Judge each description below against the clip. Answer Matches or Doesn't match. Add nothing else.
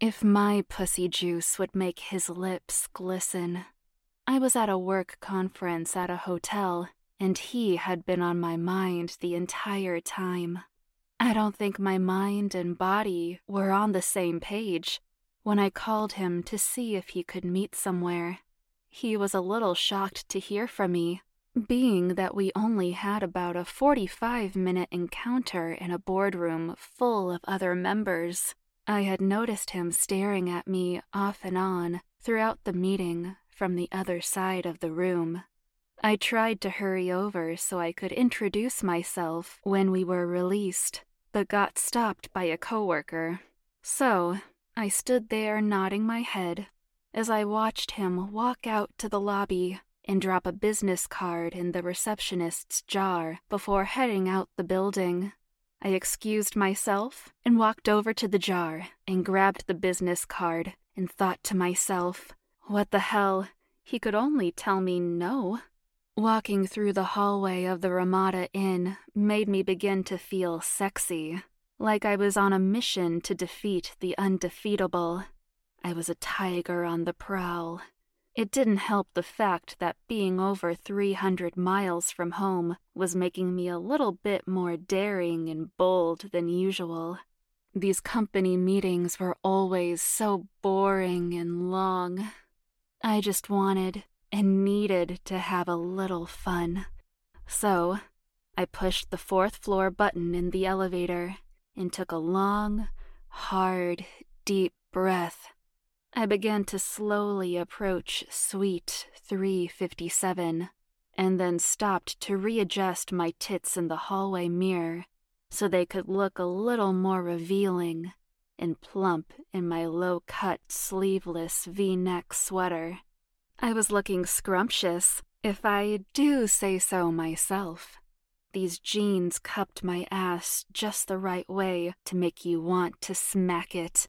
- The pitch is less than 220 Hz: Matches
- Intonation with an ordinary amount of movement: Doesn't match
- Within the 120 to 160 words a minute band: Matches